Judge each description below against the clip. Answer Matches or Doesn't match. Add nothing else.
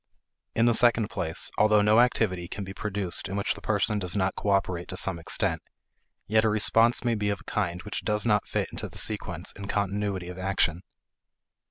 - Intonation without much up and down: Matches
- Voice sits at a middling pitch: Doesn't match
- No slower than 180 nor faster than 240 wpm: Matches